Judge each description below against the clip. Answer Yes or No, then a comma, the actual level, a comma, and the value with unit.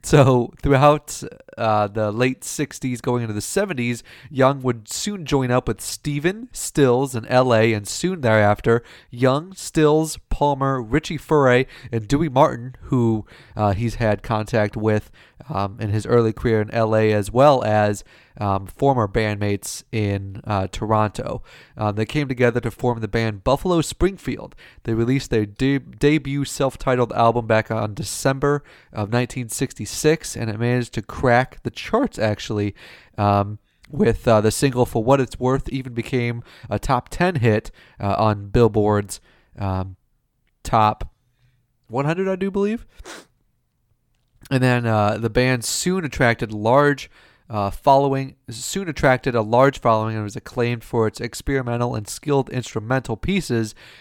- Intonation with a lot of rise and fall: No, average, 3.9 semitones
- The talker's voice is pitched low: Yes, low, 120 Hz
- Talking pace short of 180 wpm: Yes, average, 150 wpm